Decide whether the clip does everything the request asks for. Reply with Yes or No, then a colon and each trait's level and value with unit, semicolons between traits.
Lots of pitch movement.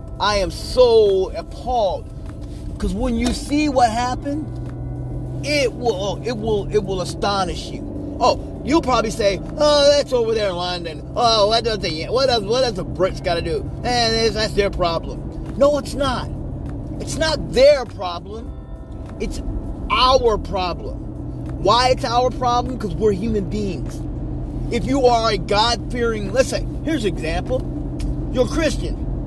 Yes: wide, 7.9 semitones